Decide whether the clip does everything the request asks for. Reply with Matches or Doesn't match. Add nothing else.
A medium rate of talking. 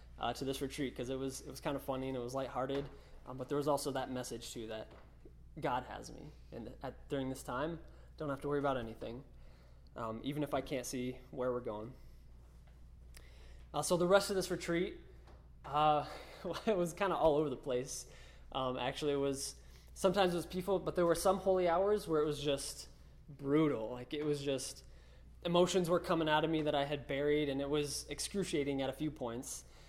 Doesn't match